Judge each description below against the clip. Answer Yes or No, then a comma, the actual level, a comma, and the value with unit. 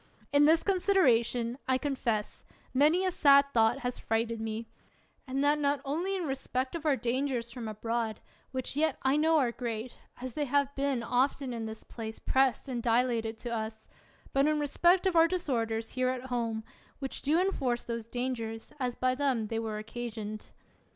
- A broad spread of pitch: No, average, 3.8 semitones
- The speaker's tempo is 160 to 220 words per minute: Yes, average, 180 wpm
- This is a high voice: Yes, very high, 255 Hz